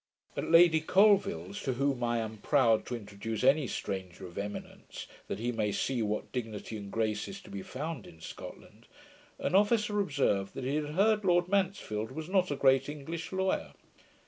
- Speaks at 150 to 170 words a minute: No, average, 180 wpm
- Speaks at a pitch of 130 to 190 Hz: Yes, low, 135 Hz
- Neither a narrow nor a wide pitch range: No, wide, 8.3 semitones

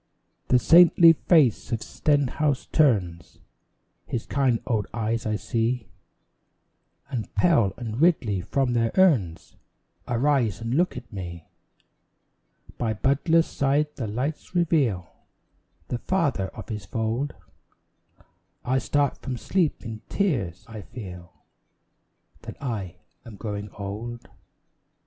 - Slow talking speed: Yes, slow, 115 wpm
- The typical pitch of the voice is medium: No, low, 120 Hz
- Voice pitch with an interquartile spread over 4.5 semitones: Yes, average, 5.1 semitones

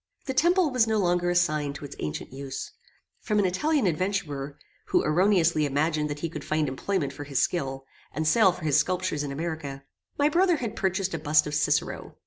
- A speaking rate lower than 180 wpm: No, average, 195 wpm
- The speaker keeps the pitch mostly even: No, average, 5.0 semitones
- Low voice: No, medium, 165 Hz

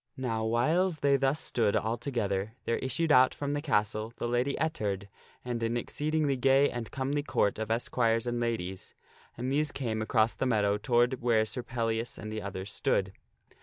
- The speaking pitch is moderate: No, low, 120 Hz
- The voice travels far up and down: No, average, 3.7 semitones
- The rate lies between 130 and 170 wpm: No, average, 180 wpm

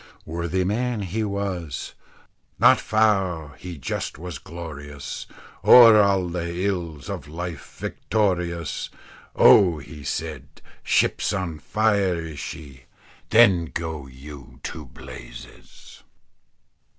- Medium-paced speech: No, slow, 105 wpm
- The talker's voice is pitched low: Yes, very low, 85 Hz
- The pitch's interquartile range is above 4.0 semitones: Yes, average, 4.5 semitones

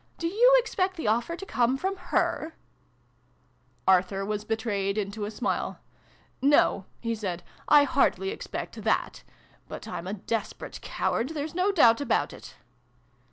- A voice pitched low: No, high, 240 Hz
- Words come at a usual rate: Yes, average, 160 wpm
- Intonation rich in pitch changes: Yes, wide, 8.6 semitones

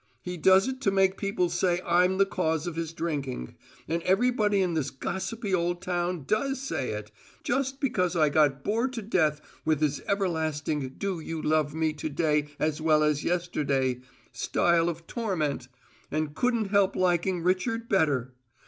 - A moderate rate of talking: Yes, average, 165 wpm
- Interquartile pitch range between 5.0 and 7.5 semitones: No, average, 4.1 semitones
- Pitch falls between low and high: Yes, medium, 175 Hz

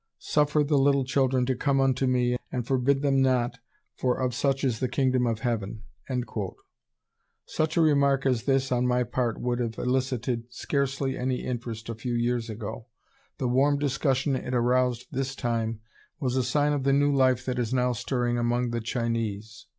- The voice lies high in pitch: No, low, 125 Hz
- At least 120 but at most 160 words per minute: No, average, 180 wpm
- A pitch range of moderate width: No, narrow, 2.1 semitones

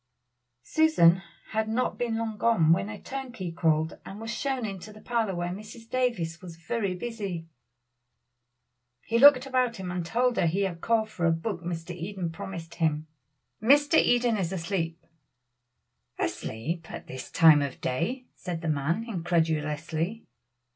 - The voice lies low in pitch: No, medium, 185 Hz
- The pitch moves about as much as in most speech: No, wide, 5.7 semitones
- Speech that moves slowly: No, average, 155 wpm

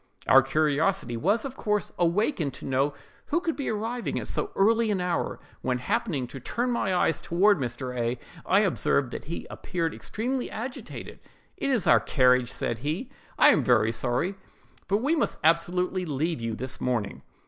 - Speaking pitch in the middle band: Yes, medium, 170 Hz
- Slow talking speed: No, average, 175 wpm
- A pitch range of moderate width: No, wide, 8.8 semitones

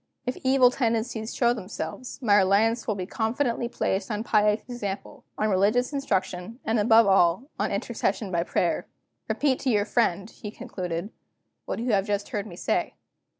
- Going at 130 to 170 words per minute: Yes, average, 165 wpm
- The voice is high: Yes, high, 215 Hz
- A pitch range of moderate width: Yes, average, 3.6 semitones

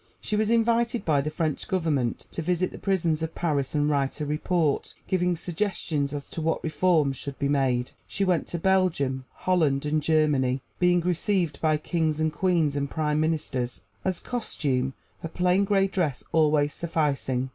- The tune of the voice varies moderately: Yes, average, 3.9 semitones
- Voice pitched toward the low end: No, medium, 155 Hz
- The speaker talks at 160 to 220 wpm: Yes, average, 170 wpm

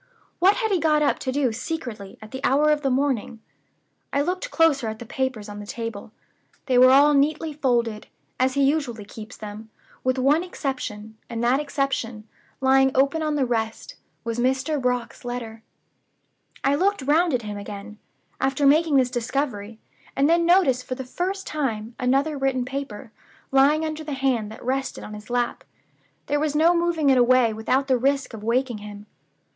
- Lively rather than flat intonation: No, average, 4.1 semitones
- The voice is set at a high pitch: Yes, very high, 265 Hz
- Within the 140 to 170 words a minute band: No, average, 180 wpm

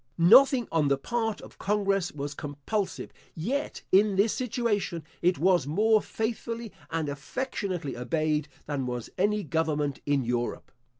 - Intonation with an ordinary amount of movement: No, wide, 6.8 semitones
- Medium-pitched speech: Yes, medium, 175 Hz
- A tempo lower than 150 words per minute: Yes, slow, 135 wpm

